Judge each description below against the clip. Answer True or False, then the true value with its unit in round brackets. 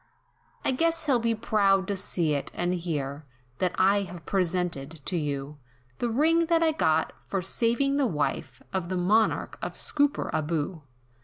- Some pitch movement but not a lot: False (6.6 semitones)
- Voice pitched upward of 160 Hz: True (190 Hz)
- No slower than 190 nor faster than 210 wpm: False (160 wpm)